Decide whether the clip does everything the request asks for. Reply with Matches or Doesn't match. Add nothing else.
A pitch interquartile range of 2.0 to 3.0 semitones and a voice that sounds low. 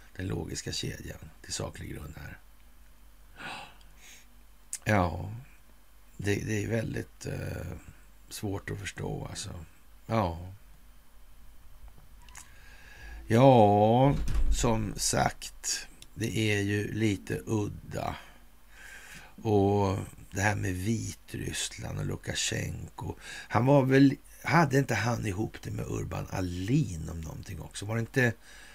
Doesn't match